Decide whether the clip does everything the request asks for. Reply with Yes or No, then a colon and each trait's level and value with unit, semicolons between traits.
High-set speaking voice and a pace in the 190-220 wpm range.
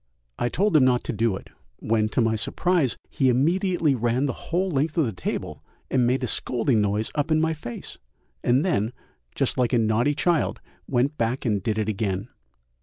No: low, 125 Hz; average, 195 wpm